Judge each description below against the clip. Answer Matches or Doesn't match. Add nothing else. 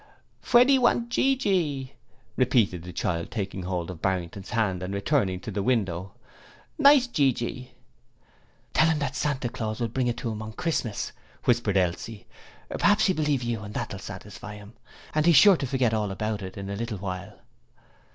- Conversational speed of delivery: Matches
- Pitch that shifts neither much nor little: Doesn't match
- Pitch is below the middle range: Matches